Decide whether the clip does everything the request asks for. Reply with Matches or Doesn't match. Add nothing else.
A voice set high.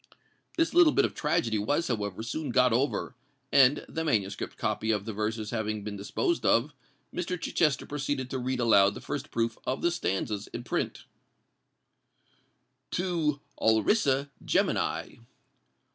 Doesn't match